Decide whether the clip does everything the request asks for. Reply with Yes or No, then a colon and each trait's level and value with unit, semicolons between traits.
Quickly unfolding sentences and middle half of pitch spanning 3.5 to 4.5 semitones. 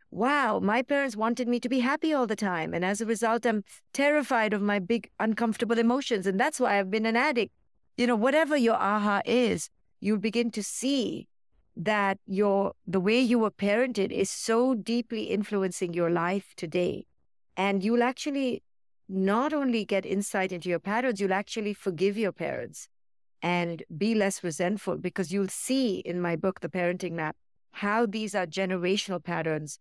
No: average, 175 wpm; average, 3.8 semitones